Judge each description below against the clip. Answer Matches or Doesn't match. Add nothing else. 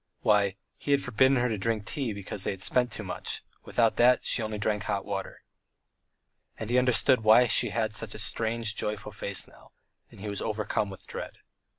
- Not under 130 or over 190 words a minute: Doesn't match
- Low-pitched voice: Matches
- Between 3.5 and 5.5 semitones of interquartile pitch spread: Doesn't match